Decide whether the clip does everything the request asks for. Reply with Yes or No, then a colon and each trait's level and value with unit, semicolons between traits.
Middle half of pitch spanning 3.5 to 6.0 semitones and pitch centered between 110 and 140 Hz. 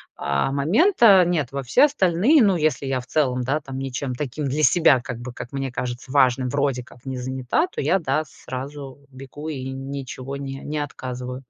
No: narrow, 2.5 semitones; low, 135 Hz